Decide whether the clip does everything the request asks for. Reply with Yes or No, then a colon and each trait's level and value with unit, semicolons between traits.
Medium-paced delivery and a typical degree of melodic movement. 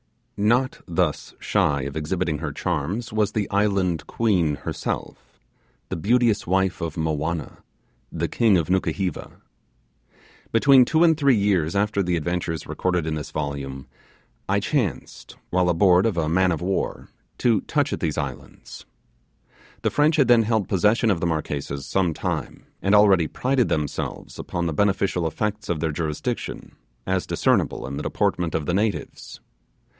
Yes: average, 155 wpm; average, 4.8 semitones